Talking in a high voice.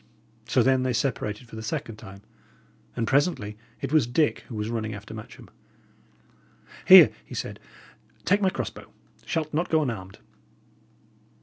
No: low, 115 Hz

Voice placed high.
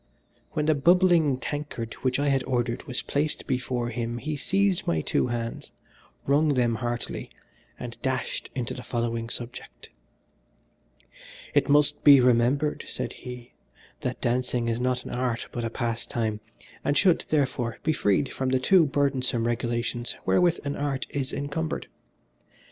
No: low, 125 Hz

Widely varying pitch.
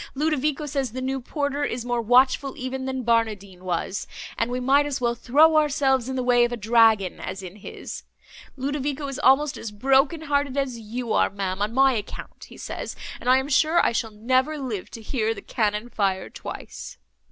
No: average, 3.7 semitones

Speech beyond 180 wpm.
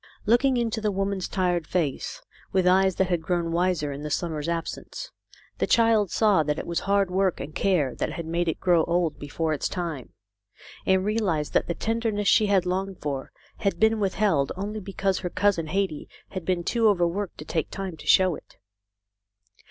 Yes: average, 190 wpm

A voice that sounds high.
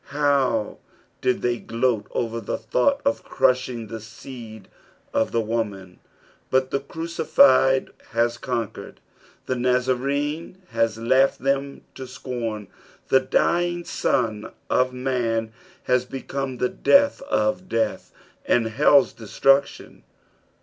No: low, 125 Hz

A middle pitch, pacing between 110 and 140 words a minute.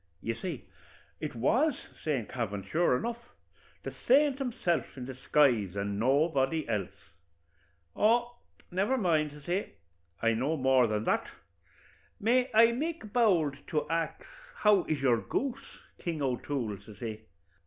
Yes: medium, 150 Hz; slow, 135 wpm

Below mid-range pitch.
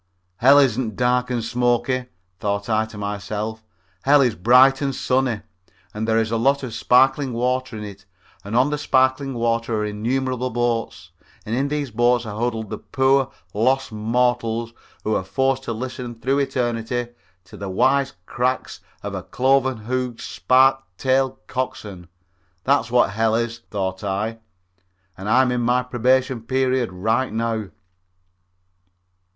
Yes: low, 120 Hz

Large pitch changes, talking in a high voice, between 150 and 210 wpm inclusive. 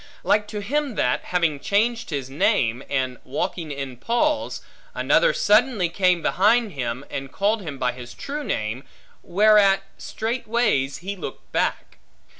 No: wide, 8.2 semitones; high, 195 Hz; average, 140 wpm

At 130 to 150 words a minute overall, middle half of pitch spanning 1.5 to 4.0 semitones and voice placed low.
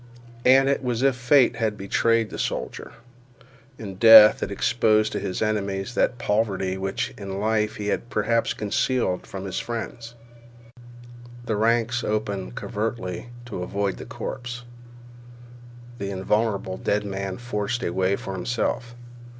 Yes: average, 140 wpm; average, 3.3 semitones; low, 110 Hz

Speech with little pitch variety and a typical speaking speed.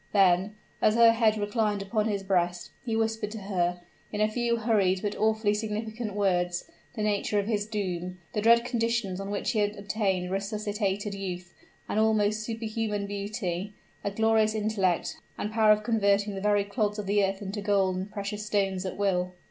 Yes: narrow, 1.9 semitones; average, 180 wpm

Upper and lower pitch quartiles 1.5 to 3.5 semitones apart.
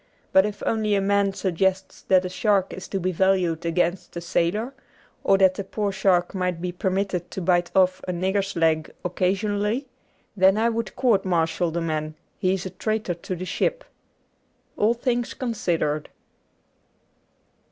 Yes: narrow, 2.5 semitones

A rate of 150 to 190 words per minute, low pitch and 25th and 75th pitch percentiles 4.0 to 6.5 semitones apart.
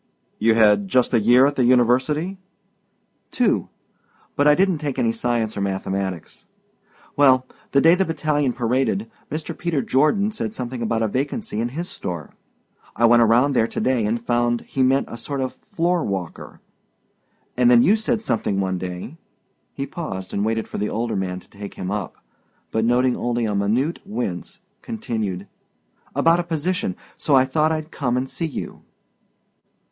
Yes: average, 175 wpm; low, 125 Hz; wide, 5.6 semitones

